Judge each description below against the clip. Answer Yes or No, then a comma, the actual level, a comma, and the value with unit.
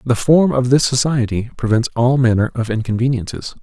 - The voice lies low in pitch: Yes, low, 125 Hz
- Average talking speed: Yes, average, 165 wpm